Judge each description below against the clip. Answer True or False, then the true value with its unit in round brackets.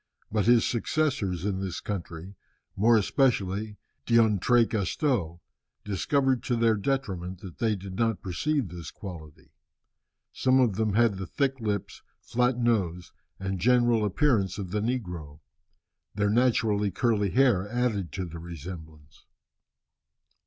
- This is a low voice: True (105 Hz)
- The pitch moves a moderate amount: True (4.5 semitones)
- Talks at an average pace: False (125 wpm)